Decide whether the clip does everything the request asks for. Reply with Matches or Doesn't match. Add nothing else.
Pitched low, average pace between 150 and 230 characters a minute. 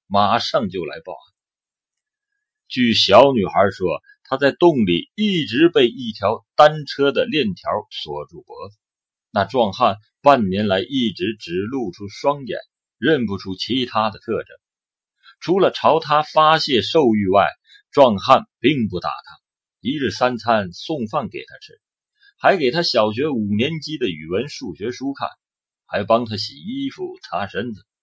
Doesn't match